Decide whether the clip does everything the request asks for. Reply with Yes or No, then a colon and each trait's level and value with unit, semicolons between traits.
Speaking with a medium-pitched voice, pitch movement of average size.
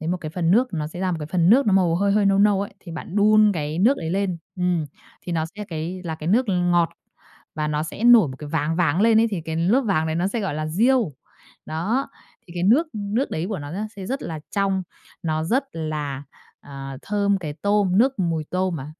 Yes: medium, 180 Hz; average, 4.4 semitones